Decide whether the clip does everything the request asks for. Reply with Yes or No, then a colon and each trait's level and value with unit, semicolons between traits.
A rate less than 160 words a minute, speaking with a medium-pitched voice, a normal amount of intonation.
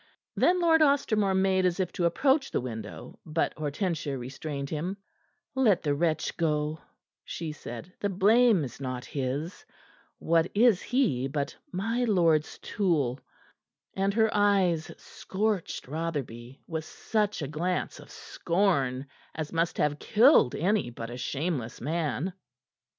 No: slow, 135 wpm; medium, 165 Hz; wide, 5.9 semitones